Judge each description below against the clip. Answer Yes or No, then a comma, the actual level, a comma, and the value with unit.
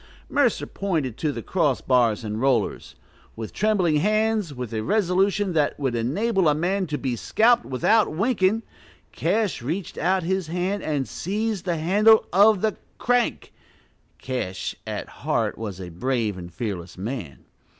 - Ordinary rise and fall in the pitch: No, wide, 8.8 semitones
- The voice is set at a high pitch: No, medium, 165 Hz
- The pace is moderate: Yes, average, 150 wpm